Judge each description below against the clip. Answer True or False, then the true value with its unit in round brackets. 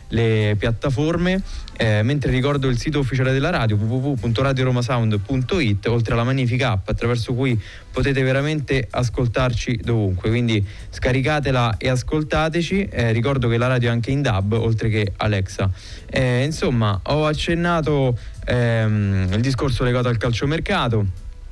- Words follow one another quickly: False (130 wpm)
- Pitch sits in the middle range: False (125 Hz)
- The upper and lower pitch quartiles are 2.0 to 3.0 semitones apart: False (3.7 semitones)